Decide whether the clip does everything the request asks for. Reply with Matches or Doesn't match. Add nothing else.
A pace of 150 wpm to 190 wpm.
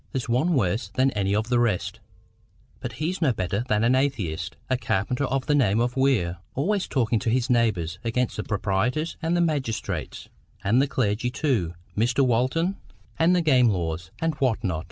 Matches